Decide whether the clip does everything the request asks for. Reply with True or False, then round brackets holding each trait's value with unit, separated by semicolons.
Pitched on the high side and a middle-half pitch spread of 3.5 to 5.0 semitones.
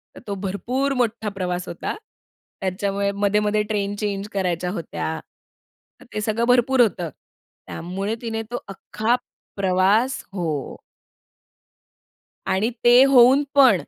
True (205 Hz; 3.9 semitones)